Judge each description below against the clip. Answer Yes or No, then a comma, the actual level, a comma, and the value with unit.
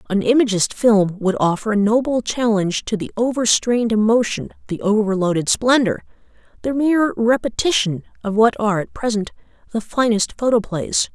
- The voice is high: Yes, high, 220 Hz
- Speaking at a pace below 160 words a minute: Yes, average, 145 wpm